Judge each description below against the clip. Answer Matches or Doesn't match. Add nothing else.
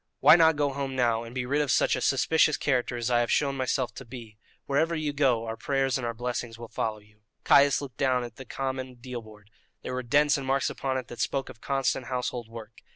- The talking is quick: Matches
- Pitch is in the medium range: Doesn't match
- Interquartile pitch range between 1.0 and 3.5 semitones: Matches